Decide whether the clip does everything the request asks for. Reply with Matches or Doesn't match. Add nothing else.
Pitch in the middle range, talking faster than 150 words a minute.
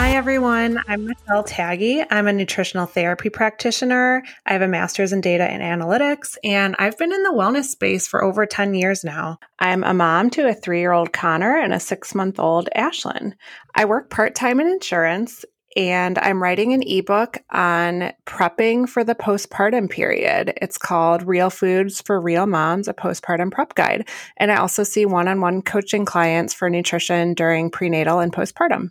Doesn't match